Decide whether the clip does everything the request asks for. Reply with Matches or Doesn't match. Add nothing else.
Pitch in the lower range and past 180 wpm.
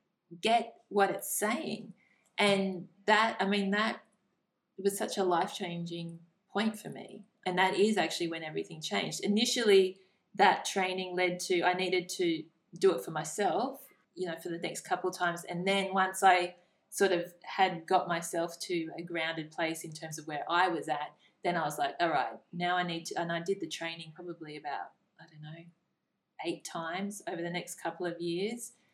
Doesn't match